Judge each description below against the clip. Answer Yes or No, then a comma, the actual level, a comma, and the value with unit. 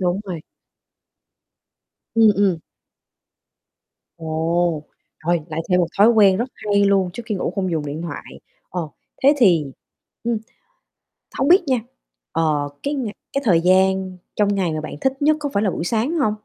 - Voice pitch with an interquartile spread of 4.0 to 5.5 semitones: Yes, average, 4.9 semitones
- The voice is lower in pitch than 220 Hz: Yes, high, 190 Hz